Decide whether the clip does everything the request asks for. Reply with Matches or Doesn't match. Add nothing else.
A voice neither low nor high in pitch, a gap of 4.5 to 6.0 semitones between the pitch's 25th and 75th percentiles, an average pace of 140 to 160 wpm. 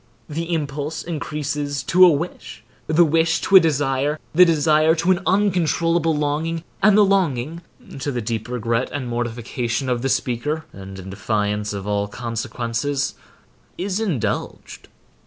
Matches